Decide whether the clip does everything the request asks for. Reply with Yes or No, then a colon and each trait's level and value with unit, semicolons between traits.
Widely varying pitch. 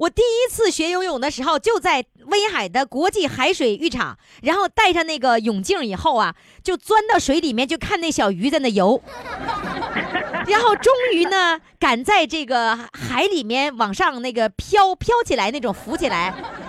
Yes: wide, 7.3 semitones